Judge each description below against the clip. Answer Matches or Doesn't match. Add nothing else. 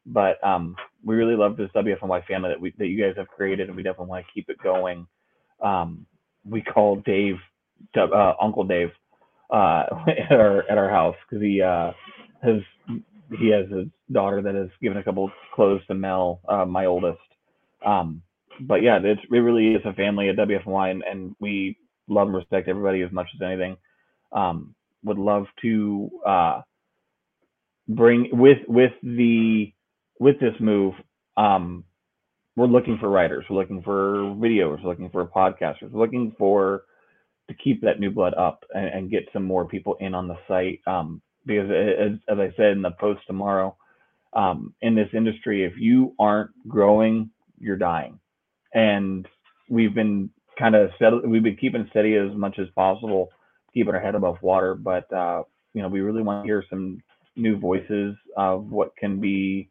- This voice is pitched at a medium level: Doesn't match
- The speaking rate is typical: Matches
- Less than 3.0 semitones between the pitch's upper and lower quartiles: Matches